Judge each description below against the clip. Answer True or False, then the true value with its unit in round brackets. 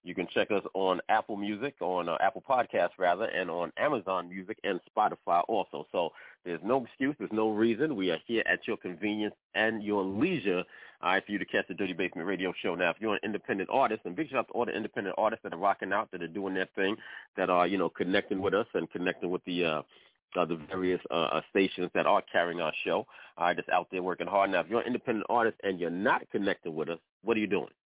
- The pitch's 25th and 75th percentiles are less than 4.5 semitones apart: True (2.9 semitones)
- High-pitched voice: False (95 Hz)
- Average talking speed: False (245 wpm)